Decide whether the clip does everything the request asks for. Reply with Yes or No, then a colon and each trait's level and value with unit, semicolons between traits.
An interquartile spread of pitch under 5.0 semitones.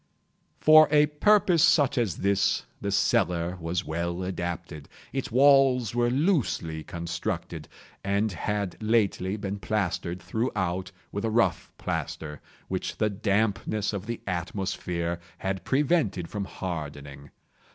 No: average, 5.3 semitones